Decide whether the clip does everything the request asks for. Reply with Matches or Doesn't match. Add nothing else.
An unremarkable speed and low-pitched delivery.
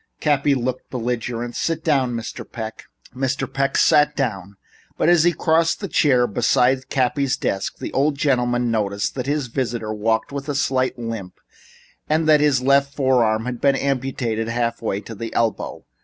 Matches